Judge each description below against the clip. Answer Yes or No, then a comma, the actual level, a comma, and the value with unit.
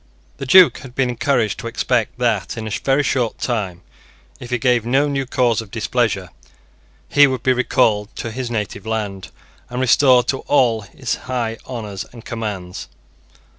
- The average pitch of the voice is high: No, low, 120 Hz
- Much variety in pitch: No, average, 2.8 semitones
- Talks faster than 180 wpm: No, average, 170 wpm